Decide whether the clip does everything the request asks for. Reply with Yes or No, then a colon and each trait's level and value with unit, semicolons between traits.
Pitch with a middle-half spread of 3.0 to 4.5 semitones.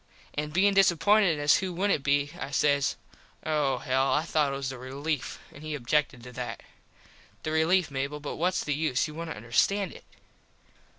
Yes: average, 3.3 semitones